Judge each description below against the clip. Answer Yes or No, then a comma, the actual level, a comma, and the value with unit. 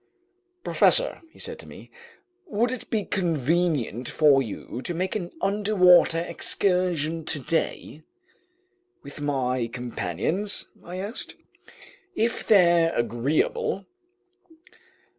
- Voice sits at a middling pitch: Yes, medium, 170 Hz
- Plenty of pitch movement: Yes, wide, 6.3 semitones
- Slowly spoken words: Yes, slow, 100 wpm